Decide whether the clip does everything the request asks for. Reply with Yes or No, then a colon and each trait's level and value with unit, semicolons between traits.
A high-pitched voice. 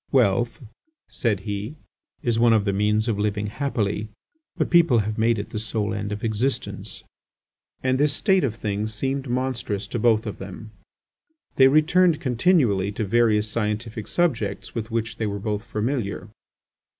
No: low, 110 Hz